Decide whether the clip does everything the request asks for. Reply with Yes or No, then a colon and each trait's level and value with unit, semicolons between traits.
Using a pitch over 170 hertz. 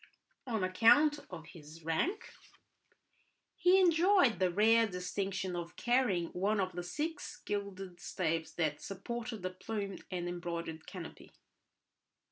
Yes: high, 190 Hz